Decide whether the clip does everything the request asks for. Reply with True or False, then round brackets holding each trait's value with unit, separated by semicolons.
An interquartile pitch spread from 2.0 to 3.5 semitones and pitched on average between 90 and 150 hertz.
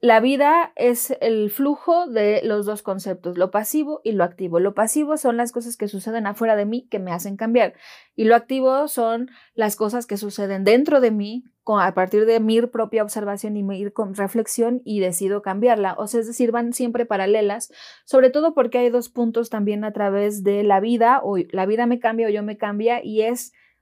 False (2.9 semitones; 220 Hz)